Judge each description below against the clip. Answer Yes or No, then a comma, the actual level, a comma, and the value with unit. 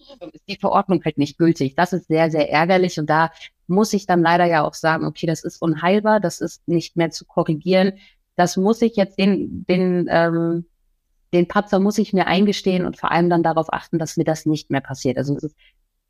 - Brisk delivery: Yes, fast, 215 wpm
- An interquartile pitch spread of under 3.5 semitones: Yes, average, 2.8 semitones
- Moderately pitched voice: Yes, medium, 170 Hz